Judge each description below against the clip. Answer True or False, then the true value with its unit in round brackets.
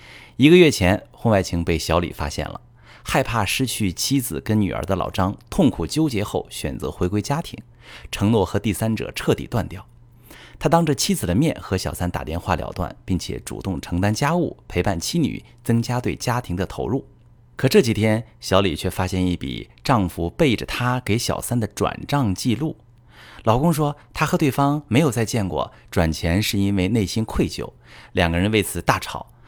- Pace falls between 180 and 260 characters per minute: False (270 characters per minute)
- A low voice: True (110 Hz)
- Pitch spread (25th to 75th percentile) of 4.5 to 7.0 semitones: True (4.9 semitones)